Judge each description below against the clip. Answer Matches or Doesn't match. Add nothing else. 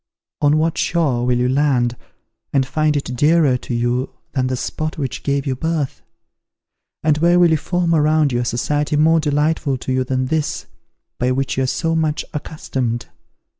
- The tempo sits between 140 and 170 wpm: Doesn't match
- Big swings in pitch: Doesn't match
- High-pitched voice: Doesn't match